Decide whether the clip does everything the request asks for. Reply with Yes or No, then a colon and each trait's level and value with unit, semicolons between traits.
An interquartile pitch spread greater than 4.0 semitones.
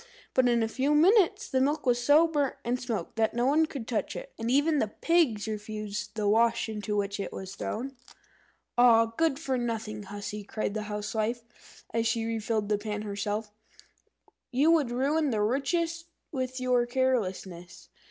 Yes: average, 4.4 semitones